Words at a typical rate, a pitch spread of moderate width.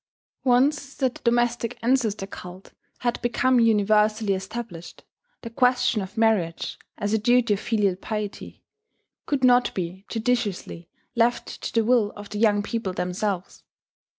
Yes: average, 145 wpm; average, 3.2 semitones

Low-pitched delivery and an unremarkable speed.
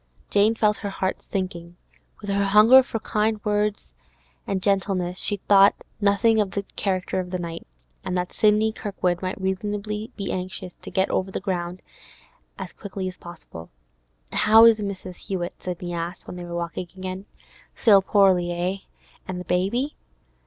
No: high, 190 Hz; average, 165 wpm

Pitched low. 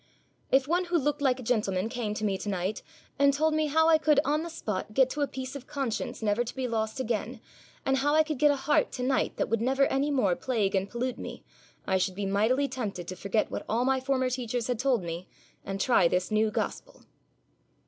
No: very high, 250 Hz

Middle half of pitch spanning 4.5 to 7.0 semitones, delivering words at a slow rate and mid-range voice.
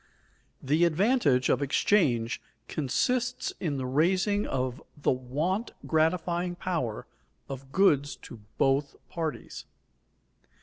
Yes: wide, 5.5 semitones; slow, 100 wpm; medium, 155 Hz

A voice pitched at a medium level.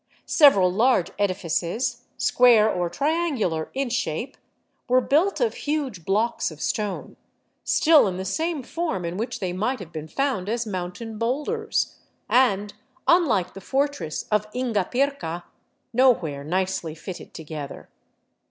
No: high, 215 Hz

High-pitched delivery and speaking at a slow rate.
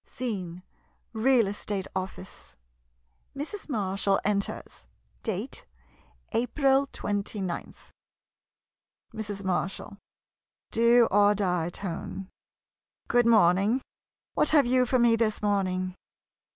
Yes: high, 205 Hz; slow, 100 wpm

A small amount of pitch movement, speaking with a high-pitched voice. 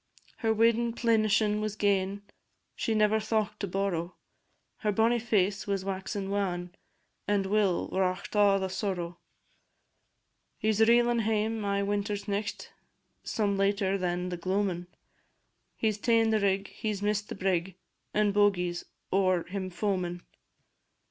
Yes: narrow, 2.2 semitones; high, 200 Hz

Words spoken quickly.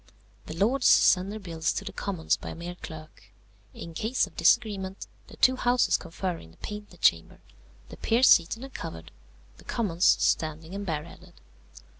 No: average, 170 wpm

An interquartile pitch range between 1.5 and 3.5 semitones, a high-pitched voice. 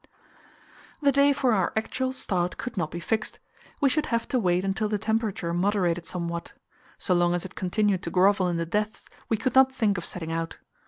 No: average, 4.3 semitones; high, 195 Hz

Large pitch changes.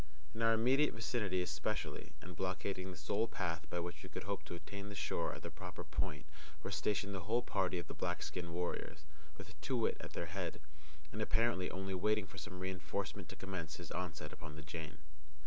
No: average, 2.8 semitones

